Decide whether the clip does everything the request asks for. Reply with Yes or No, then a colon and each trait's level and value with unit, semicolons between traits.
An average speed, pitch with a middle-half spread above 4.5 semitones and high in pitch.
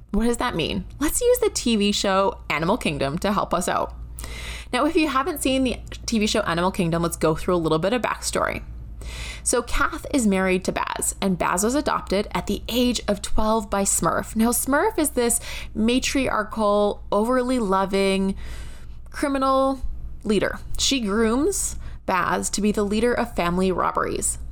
Yes: average, 170 wpm; average, 5.2 semitones; high, 210 Hz